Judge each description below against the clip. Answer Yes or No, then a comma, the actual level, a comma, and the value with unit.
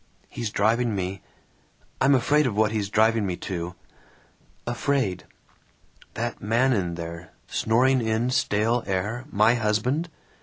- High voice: No, low, 110 Hz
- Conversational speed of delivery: No, slow, 125 wpm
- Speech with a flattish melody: No, average, 3.7 semitones